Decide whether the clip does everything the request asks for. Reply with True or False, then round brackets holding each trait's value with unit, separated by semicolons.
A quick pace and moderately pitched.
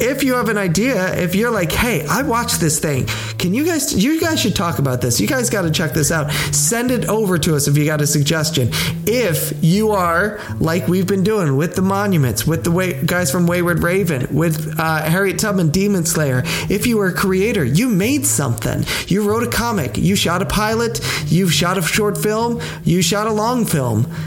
True (220 wpm; 175 Hz)